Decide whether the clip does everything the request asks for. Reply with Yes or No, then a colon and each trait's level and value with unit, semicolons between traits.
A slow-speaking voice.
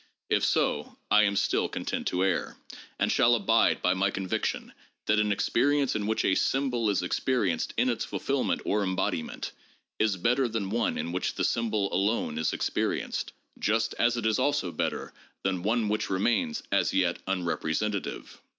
No: average, 170 wpm